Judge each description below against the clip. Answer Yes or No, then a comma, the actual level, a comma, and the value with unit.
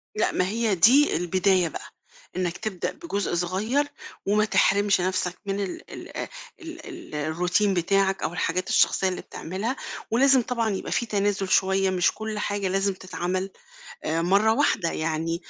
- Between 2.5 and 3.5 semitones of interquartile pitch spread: Yes, average, 3.0 semitones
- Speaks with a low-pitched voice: No, high, 195 Hz